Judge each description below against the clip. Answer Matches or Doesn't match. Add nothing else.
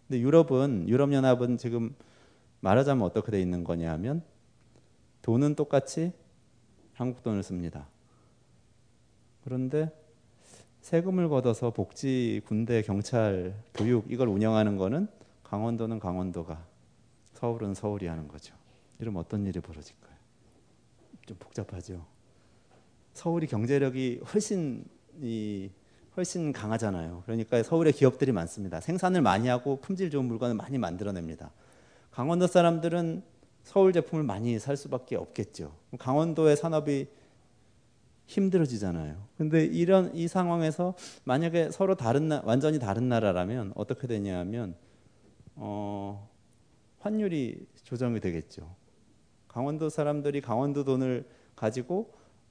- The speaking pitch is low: Matches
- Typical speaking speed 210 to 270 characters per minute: Doesn't match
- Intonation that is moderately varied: Doesn't match